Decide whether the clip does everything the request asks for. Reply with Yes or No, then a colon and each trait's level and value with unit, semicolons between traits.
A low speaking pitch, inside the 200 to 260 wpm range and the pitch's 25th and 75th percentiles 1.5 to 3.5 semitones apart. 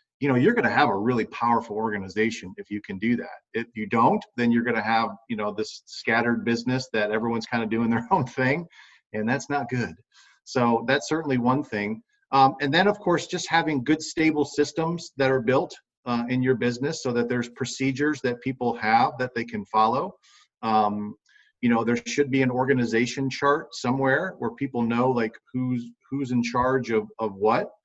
Yes: low, 125 Hz; fast, 205 wpm; average, 2.9 semitones